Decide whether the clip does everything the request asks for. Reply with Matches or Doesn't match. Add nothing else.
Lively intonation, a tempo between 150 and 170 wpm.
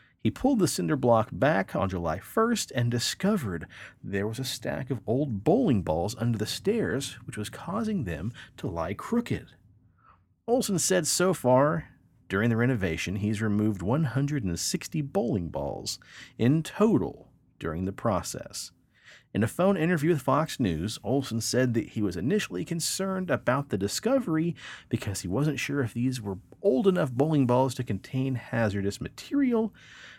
Matches